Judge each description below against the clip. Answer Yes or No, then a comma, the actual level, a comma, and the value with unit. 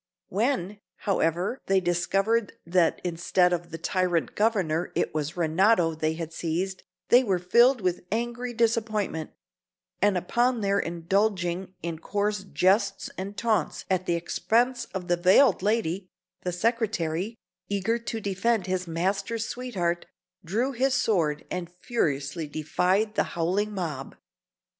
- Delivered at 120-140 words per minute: Yes, slow, 135 wpm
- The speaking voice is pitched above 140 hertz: Yes, high, 190 Hz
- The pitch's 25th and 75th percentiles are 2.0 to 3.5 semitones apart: No, average, 4.4 semitones